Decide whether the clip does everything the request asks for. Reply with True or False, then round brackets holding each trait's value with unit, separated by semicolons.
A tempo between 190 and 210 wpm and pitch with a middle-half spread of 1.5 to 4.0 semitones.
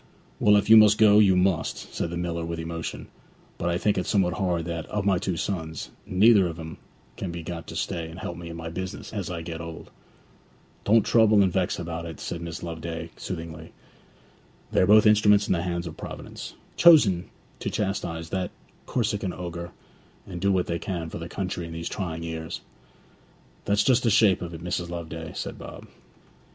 True (200 wpm; 3.1 semitones)